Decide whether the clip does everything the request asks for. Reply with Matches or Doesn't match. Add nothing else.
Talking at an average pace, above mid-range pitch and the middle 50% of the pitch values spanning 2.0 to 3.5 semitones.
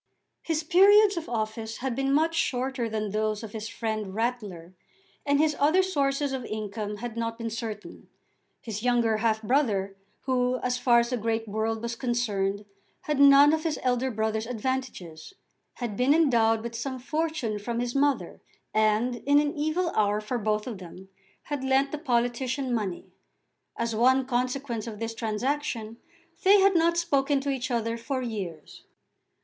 Doesn't match